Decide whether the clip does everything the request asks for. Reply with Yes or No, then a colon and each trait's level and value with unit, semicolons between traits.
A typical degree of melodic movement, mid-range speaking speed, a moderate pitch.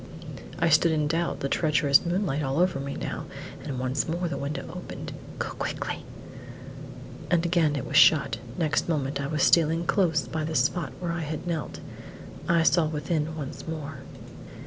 Yes: average, 3.1 semitones; average, 170 wpm; medium, 155 Hz